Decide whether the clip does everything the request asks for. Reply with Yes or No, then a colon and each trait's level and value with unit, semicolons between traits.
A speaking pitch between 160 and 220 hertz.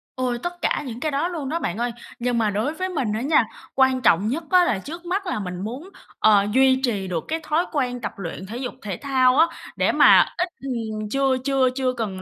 No: very high, 255 Hz